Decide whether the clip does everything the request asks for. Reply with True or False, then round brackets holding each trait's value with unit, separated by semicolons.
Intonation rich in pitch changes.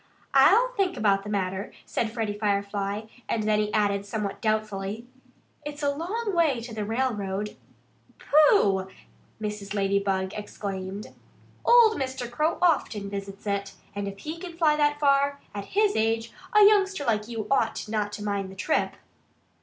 True (6.4 semitones)